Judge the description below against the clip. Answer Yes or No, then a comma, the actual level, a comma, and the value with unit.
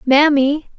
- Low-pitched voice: No, very high, 285 Hz